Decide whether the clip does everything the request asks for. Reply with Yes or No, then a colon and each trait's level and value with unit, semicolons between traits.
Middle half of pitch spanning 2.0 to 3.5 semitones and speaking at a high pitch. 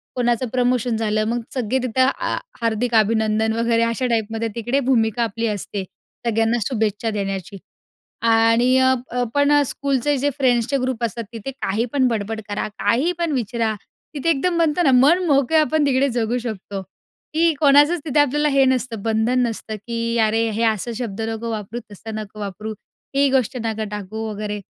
Yes: average, 3.2 semitones; high, 235 Hz